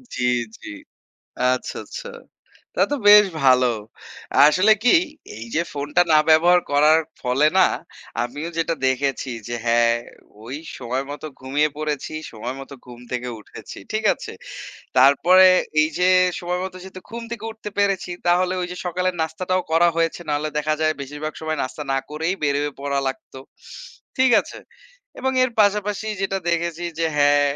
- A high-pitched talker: No, medium, 155 Hz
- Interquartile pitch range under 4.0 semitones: No, average, 4.7 semitones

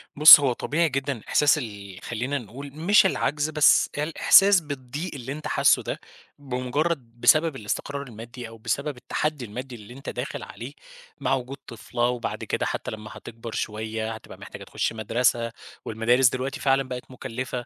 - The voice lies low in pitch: Yes, low, 130 Hz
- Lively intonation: No, average, 3.7 semitones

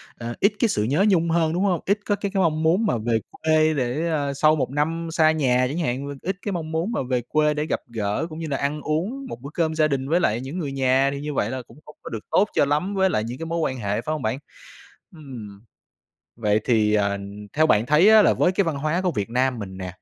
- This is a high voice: No, medium, 150 Hz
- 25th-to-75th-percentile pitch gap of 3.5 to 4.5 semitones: No, average, 5.1 semitones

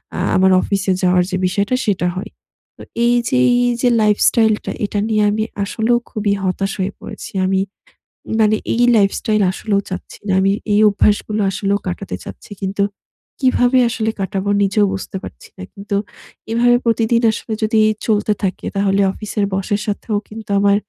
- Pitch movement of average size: No, narrow, 2.1 semitones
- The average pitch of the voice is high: Yes, high, 205 Hz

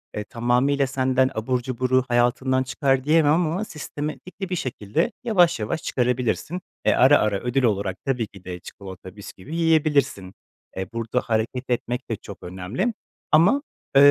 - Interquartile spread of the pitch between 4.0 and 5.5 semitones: Yes, average, 5.1 semitones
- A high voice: No, low, 130 Hz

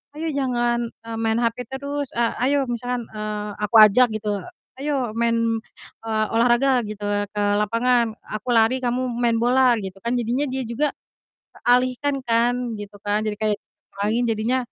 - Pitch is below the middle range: No, high, 235 Hz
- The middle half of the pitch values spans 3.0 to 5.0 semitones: No, narrow, 2.6 semitones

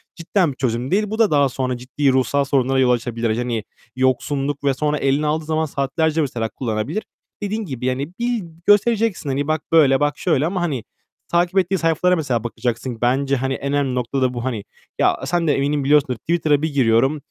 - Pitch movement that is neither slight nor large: Yes, average, 3.8 semitones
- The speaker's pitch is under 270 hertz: Yes, medium, 140 Hz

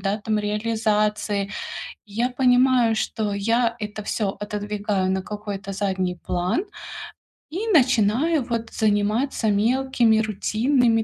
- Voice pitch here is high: Yes, high, 215 Hz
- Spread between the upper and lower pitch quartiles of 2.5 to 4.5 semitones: Yes, average, 2.8 semitones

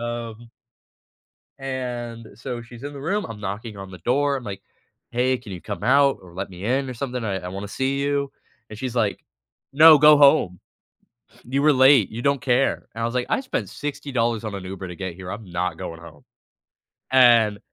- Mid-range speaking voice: No, low, 120 Hz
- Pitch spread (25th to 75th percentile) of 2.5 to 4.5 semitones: No, average, 5.2 semitones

